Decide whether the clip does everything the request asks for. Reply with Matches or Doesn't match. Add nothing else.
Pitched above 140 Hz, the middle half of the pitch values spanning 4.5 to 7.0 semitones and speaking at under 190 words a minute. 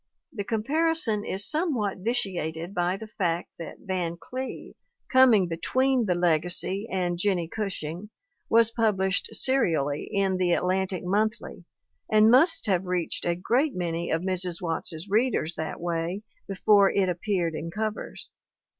Doesn't match